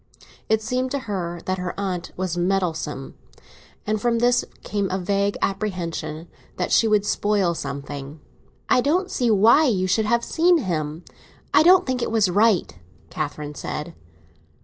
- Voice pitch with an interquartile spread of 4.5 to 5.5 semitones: Yes, average, 5.1 semitones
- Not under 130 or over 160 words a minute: Yes, average, 155 wpm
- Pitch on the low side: No, high, 195 Hz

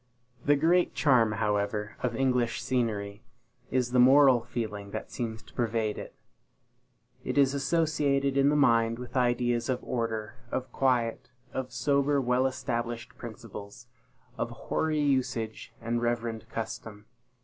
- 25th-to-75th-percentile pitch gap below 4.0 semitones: Yes, average, 2.9 semitones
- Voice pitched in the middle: No, low, 120 Hz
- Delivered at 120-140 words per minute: Yes, slow, 135 wpm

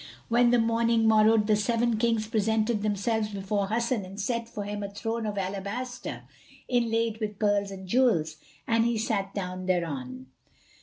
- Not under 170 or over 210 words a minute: No, average, 160 wpm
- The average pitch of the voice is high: Yes, high, 215 Hz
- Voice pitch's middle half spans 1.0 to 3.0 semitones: Yes, narrow, 2.6 semitones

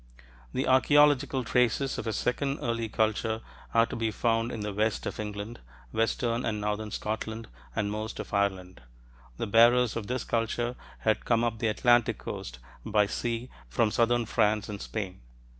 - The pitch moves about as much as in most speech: No, narrow, 2.0 semitones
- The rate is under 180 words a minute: Yes, average, 165 wpm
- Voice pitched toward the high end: No, low, 115 Hz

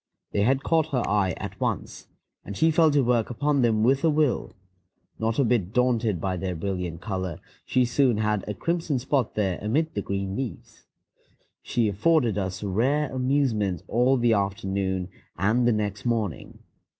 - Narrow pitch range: No, average, 5.2 semitones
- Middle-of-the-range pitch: No, low, 110 Hz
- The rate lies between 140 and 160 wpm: No, average, 170 wpm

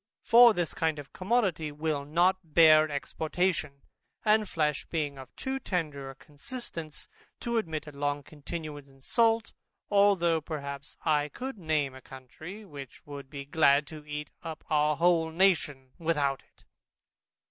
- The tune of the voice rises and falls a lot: No, average, 3.7 semitones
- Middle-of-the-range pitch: Yes, medium, 155 Hz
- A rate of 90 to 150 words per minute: Yes, average, 145 wpm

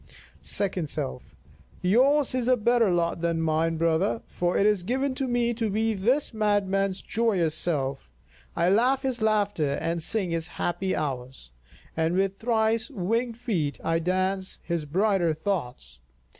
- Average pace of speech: Yes, average, 150 wpm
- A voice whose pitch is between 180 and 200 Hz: Yes, high, 190 Hz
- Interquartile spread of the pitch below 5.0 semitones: No, wide, 5.4 semitones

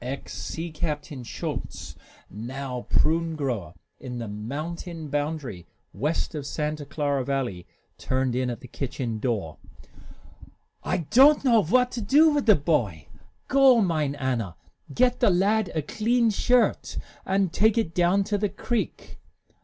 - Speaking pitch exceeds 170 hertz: No, medium, 155 Hz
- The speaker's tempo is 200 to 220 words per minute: No, average, 145 wpm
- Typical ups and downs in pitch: No, wide, 7.7 semitones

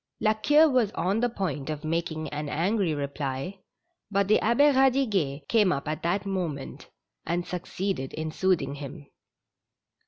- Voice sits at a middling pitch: Yes, medium, 175 Hz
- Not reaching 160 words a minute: Yes, average, 150 wpm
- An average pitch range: No, wide, 6.1 semitones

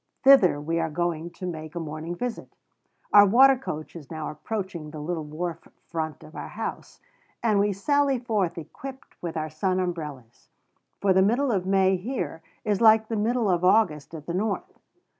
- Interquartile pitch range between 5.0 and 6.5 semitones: Yes, wide, 5.5 semitones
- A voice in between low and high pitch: Yes, medium, 180 Hz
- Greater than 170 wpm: Yes, average, 180 wpm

